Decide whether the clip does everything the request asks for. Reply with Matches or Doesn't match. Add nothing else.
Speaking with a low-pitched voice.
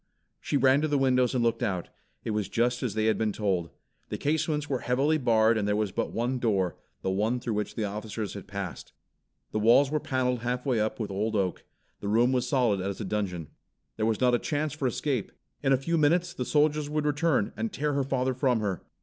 Matches